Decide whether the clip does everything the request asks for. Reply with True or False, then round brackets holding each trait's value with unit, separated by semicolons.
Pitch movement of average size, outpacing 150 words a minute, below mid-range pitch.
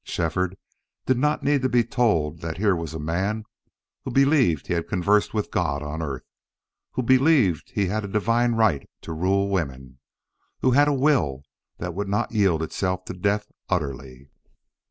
False (6.3 semitones; 175 wpm; 95 Hz)